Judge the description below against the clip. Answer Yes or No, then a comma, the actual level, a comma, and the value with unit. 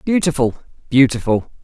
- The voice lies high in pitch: No, low, 135 Hz